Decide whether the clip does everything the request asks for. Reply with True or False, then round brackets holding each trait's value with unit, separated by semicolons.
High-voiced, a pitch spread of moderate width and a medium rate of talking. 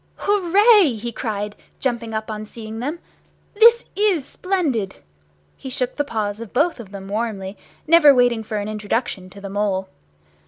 False (230 Hz; 6.2 semitones; 160 wpm)